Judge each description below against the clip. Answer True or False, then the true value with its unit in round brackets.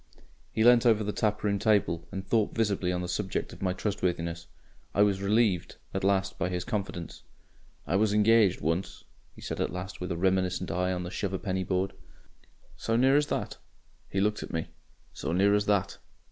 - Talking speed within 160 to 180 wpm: False (190 wpm)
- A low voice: True (95 Hz)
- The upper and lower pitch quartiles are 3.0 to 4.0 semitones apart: False (2.5 semitones)